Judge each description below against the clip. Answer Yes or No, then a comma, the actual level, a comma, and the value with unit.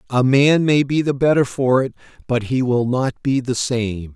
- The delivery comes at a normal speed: No, fast, 215 wpm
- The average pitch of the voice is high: No, low, 130 Hz